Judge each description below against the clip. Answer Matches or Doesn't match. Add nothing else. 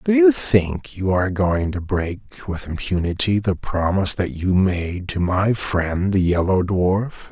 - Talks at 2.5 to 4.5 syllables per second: Matches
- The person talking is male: Matches